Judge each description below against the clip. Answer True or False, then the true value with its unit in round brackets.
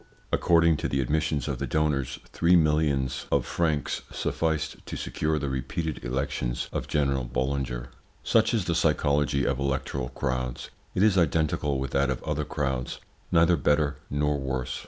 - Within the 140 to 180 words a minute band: True (155 wpm)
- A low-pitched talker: True (70 Hz)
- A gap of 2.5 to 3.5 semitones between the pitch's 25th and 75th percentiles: True (2.9 semitones)